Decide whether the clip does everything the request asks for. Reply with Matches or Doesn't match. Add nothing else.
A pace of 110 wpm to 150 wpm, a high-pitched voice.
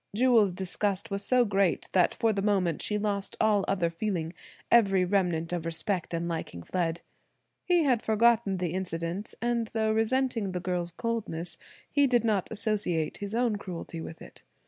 Doesn't match